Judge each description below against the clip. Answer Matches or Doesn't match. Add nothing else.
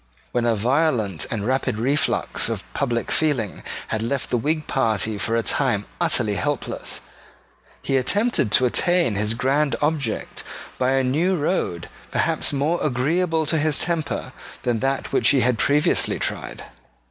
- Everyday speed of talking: Matches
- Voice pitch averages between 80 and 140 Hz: Matches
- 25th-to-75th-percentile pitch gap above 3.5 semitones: Matches